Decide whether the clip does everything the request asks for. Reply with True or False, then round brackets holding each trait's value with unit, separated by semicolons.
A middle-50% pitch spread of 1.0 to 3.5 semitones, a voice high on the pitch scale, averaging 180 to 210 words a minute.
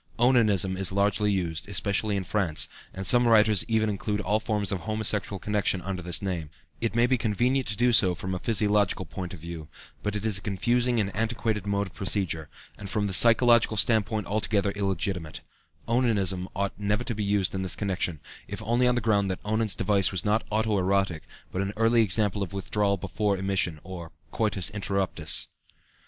False (2.5 semitones; 100 Hz; 190 wpm)